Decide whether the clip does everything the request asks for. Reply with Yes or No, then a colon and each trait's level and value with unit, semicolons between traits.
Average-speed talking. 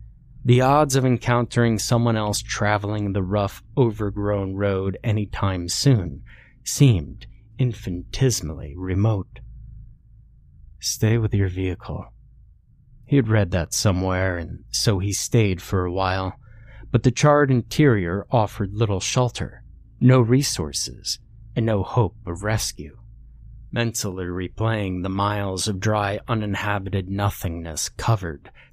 No: slow, 115 wpm